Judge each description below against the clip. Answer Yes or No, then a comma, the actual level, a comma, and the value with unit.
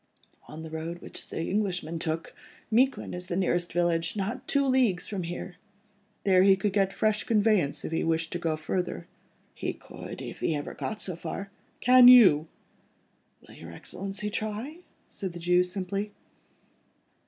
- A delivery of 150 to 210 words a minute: Yes, average, 160 wpm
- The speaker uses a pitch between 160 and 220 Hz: Yes, medium, 185 Hz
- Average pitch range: Yes, average, 3.9 semitones